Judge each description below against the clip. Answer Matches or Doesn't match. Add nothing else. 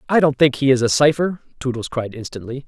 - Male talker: Matches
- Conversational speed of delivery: Doesn't match